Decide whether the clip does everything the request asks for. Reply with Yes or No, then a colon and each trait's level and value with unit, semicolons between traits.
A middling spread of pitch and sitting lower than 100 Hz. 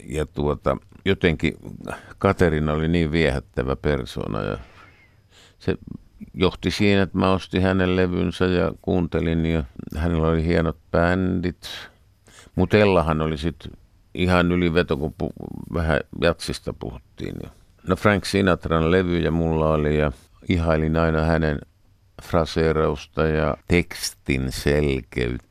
Yes: average, 3.0 semitones; very low, 85 Hz